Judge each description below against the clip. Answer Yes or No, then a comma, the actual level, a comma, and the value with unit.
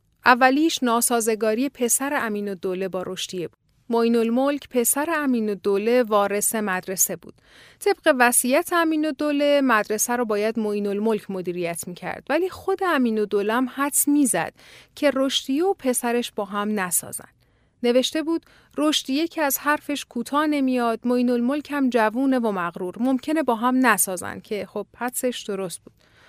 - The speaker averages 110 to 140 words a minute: No, fast, 155 wpm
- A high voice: Yes, high, 240 Hz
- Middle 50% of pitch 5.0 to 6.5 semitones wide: Yes, average, 5.3 semitones